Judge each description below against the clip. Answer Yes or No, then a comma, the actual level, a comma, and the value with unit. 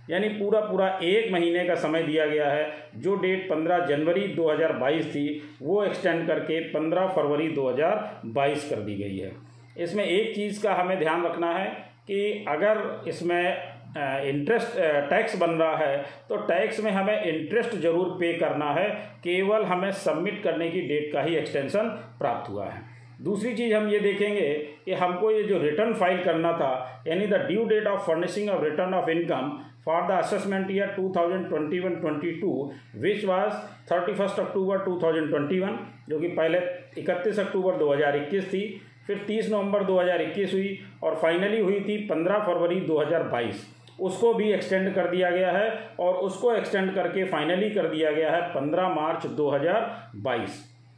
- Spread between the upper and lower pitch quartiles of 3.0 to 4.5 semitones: Yes, average, 4.2 semitones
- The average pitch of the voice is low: No, medium, 180 Hz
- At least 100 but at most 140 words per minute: No, average, 160 wpm